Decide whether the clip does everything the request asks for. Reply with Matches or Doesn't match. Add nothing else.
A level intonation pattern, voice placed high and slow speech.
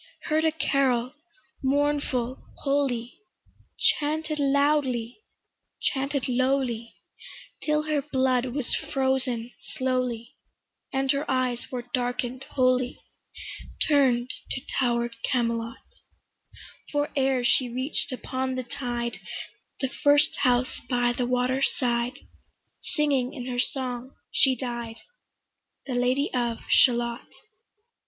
Matches